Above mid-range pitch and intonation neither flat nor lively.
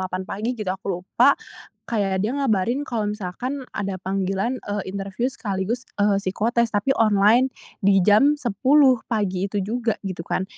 Yes: high, 205 Hz; average, 3.8 semitones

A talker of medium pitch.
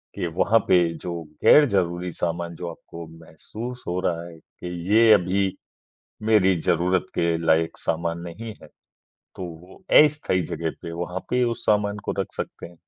No: very low, 90 Hz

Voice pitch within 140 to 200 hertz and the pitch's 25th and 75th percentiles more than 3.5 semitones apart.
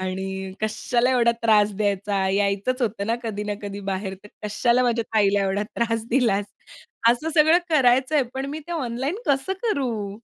No: high, 225 Hz; average, 4.2 semitones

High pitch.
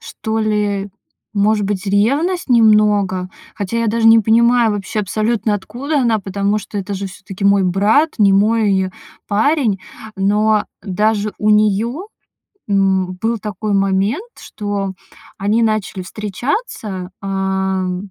Yes: high, 210 Hz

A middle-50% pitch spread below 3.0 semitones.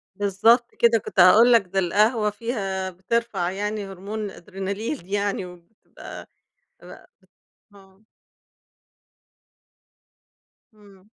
Yes: narrow, 2.4 semitones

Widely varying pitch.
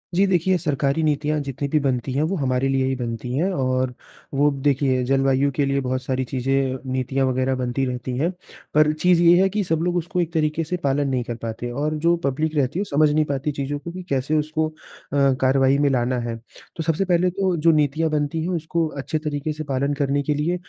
No: average, 3.1 semitones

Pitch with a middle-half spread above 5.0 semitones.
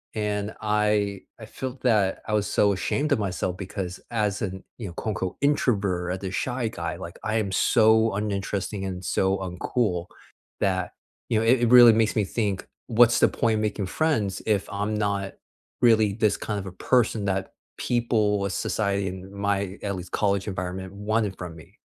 No: narrow, 2.5 semitones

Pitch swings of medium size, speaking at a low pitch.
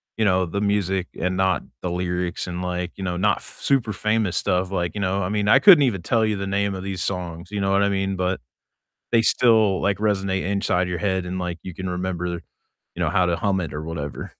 No: narrow, 2.1 semitones; very low, 95 Hz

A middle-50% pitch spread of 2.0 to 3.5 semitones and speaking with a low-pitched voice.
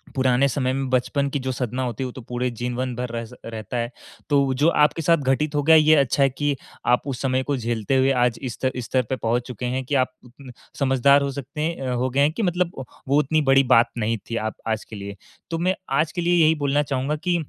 Yes: average, 2.8 semitones; low, 130 Hz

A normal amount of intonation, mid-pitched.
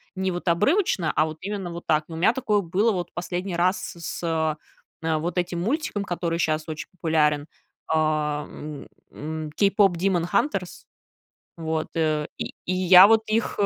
Yes: average, 3.4 semitones; medium, 175 Hz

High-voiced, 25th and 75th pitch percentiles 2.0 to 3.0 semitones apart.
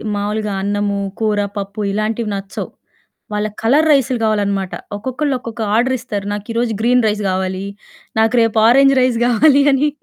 No: high, 220 Hz; average, 3.4 semitones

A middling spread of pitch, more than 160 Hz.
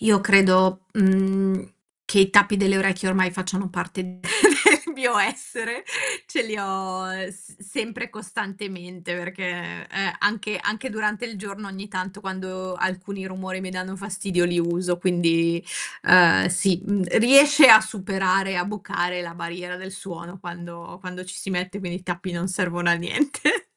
No: narrow, 1.9 semitones; high, 190 Hz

